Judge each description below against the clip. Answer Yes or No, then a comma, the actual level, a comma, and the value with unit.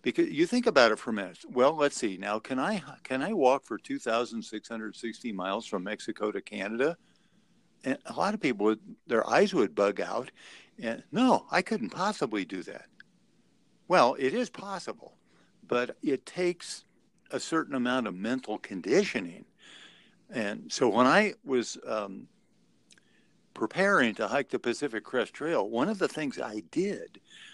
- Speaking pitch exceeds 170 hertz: No, medium, 140 Hz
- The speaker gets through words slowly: No, average, 160 wpm